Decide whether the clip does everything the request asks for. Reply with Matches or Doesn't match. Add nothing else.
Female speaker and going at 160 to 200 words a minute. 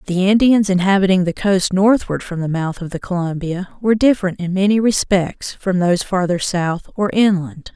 Matches